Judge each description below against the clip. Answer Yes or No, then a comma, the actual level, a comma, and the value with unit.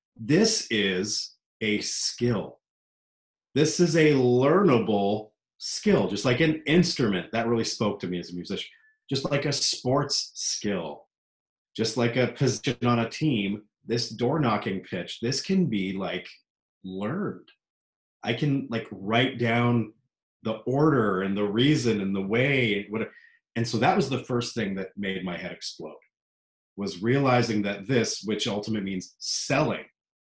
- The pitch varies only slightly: No, average, 5.0 semitones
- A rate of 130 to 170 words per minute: Yes, average, 150 wpm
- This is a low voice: Yes, low, 115 Hz